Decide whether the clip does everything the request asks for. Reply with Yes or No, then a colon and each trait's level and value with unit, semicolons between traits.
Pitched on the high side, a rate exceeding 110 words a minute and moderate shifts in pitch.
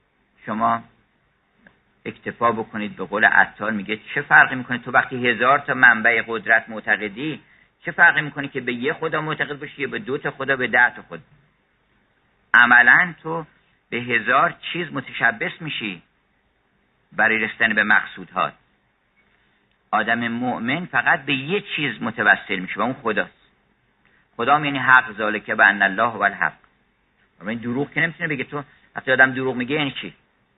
No: low, 130 Hz; average, 150 wpm; average, 4.1 semitones